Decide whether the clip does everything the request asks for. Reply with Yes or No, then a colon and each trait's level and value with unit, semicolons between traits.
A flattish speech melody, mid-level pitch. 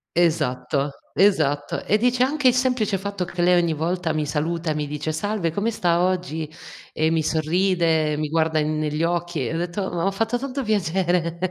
No: average, 3.8 semitones; medium, 170 Hz